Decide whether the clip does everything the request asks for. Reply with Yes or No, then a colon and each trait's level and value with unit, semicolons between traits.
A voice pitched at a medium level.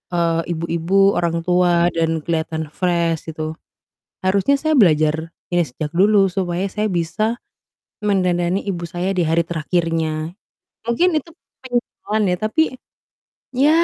Yes: medium, 175 Hz